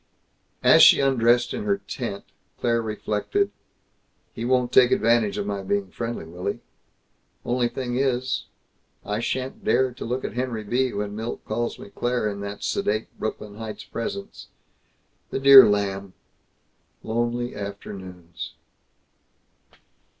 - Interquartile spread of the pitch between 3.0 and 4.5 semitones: Yes, average, 3.5 semitones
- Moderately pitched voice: No, low, 115 Hz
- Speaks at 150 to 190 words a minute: No, slow, 135 wpm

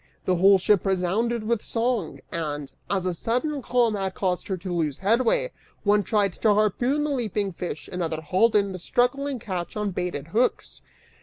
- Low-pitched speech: No, high, 200 Hz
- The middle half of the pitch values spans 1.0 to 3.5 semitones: No, average, 4.6 semitones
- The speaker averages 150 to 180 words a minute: Yes, average, 175 wpm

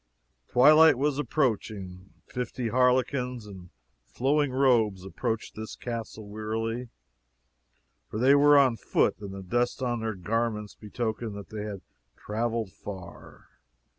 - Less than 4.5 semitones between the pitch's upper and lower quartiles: Yes, average, 3.2 semitones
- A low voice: Yes, low, 115 Hz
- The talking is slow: Yes, slow, 125 wpm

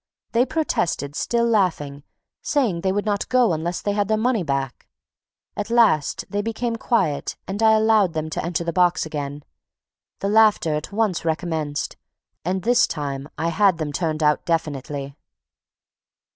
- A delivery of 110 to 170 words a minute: Yes, average, 160 wpm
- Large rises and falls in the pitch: Yes, wide, 5.9 semitones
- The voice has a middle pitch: Yes, medium, 175 Hz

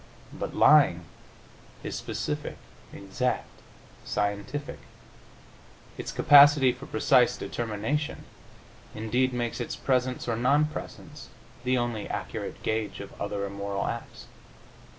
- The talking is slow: Yes, slow, 105 wpm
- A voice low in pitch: Yes, low, 120 Hz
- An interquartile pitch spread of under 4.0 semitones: No, average, 4.4 semitones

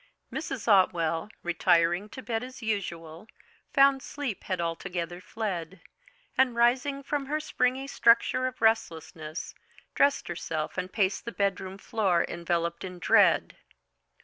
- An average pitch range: No, wide, 6.5 semitones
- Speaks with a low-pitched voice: No, high, 200 Hz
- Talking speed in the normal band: No, slow, 125 wpm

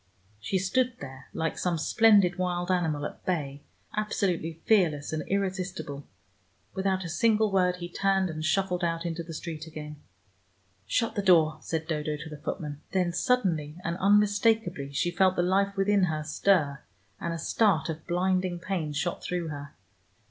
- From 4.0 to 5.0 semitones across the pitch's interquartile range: No, average, 3.6 semitones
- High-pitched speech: No, medium, 175 Hz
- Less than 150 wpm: No, average, 165 wpm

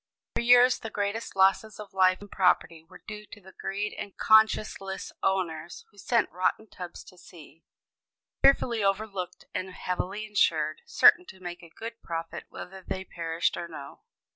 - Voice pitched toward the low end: No, high, 190 Hz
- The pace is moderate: Yes, average, 165 wpm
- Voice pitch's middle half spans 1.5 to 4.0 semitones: Yes, average, 3.3 semitones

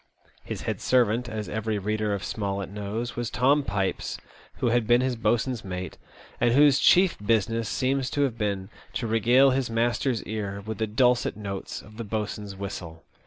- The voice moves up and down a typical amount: Yes, average, 3.2 semitones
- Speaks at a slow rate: No, average, 175 wpm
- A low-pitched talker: Yes, low, 110 Hz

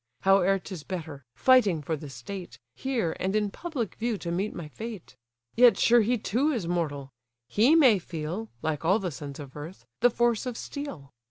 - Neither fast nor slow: Yes, average, 185 wpm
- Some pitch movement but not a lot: No, wide, 6.7 semitones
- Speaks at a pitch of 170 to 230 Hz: Yes, high, 190 Hz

